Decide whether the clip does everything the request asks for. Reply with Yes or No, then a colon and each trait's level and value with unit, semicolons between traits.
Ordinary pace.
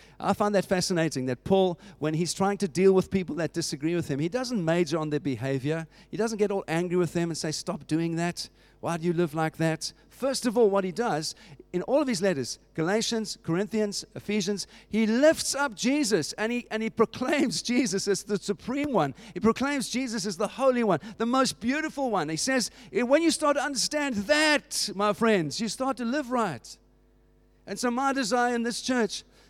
No: fast, 210 wpm